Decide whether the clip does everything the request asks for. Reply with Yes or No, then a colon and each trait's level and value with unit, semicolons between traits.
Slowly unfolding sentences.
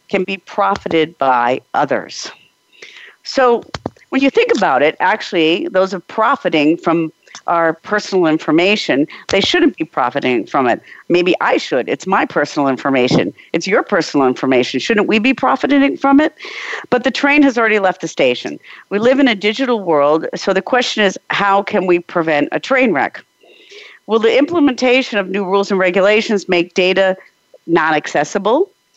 No: average, 165 wpm